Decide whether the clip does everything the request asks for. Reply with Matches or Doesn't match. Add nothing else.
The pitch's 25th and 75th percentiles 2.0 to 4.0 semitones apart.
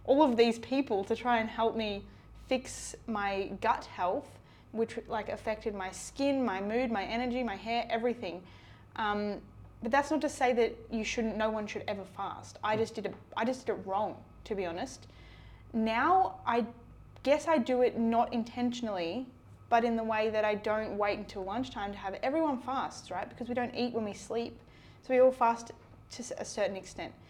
Matches